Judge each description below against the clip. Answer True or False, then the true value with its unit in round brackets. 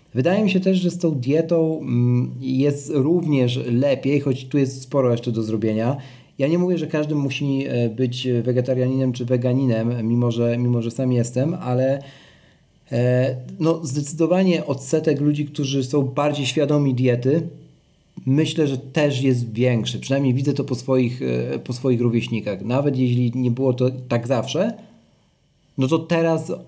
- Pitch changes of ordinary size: True (3.1 semitones)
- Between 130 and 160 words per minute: True (150 wpm)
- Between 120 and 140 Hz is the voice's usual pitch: True (135 Hz)